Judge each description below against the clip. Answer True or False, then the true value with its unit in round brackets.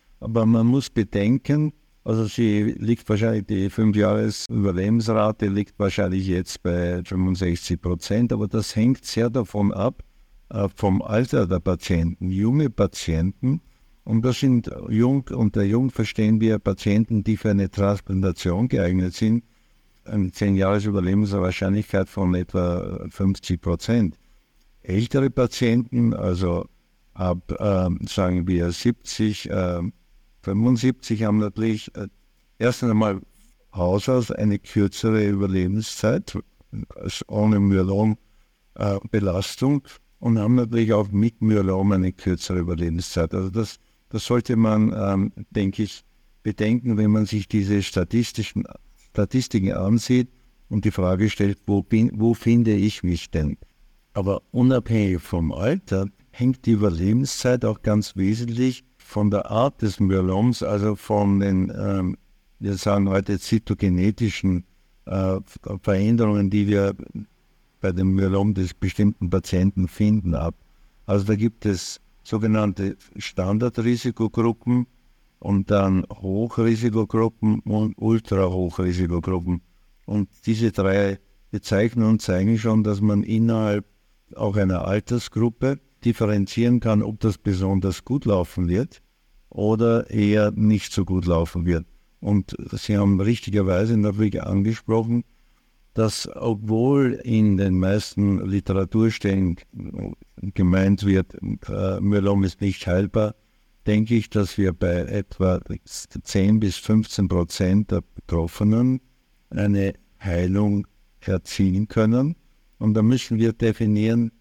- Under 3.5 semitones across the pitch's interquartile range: True (2.9 semitones)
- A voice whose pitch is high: False (105 Hz)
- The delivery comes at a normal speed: False (120 wpm)